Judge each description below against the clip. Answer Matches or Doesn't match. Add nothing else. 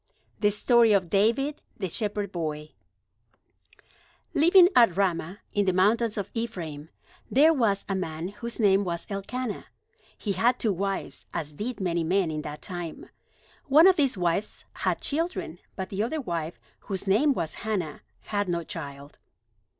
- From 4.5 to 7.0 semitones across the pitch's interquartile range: Matches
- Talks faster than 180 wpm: Doesn't match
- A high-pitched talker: Matches